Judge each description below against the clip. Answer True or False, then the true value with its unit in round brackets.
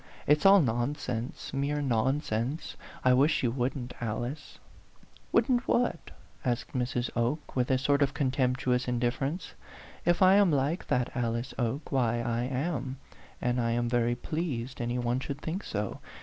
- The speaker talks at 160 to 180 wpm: False (150 wpm)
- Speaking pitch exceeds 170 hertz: False (130 Hz)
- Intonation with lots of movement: False (3.3 semitones)